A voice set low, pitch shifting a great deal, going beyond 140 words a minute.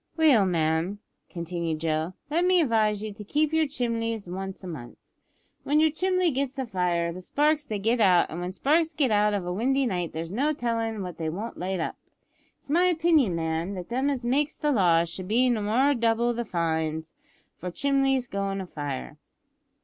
No: high, 215 Hz; wide, 7.6 semitones; average, 190 wpm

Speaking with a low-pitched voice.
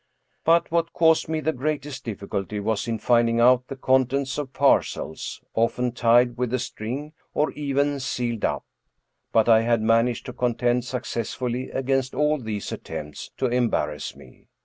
Yes: low, 125 Hz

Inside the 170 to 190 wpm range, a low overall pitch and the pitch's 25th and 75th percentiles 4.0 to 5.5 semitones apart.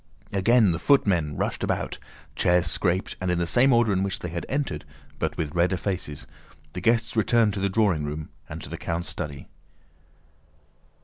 Yes: average, 180 wpm; very low, 95 Hz; average, 4.6 semitones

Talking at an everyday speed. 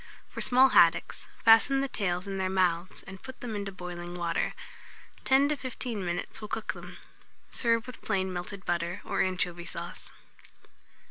Yes: average, 160 wpm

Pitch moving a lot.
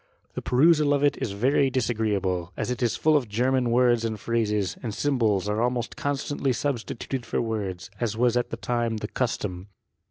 No: average, 3.6 semitones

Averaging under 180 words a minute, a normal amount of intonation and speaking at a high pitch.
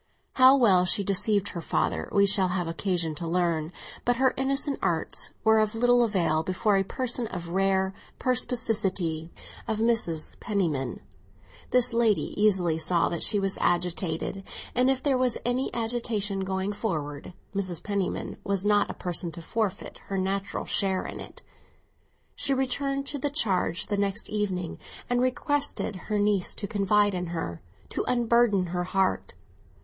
Yes: average, 155 wpm; average, 4.6 semitones; high, 200 Hz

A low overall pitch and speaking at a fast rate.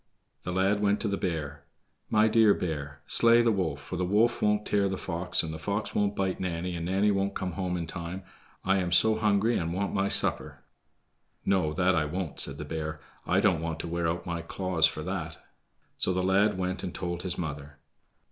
Yes: very low, 90 Hz; fast, 215 wpm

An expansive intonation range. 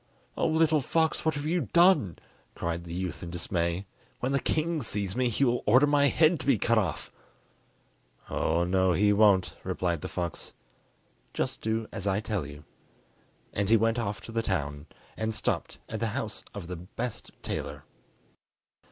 Yes: wide, 6.8 semitones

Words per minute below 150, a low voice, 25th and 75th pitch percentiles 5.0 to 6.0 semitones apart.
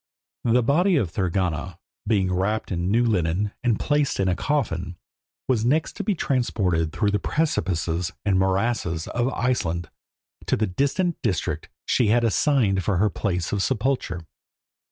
No: average, 155 wpm; low, 105 Hz; wide, 5.5 semitones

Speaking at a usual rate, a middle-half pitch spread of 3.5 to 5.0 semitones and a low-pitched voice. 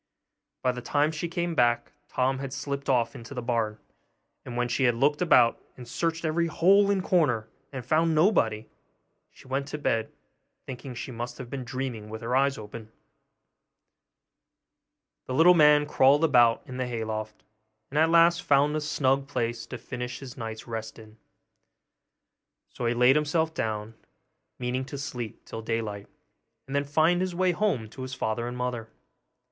Yes: average, 175 wpm; average, 4.3 semitones; low, 130 Hz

